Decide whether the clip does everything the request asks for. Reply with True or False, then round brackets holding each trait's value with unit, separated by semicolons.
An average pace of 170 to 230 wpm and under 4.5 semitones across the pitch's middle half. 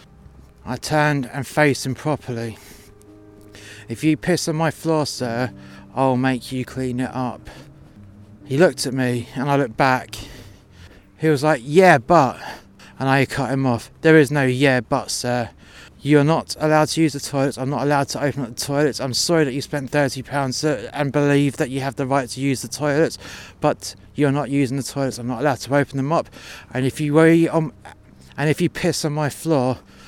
True (200 wpm; 3.7 semitones)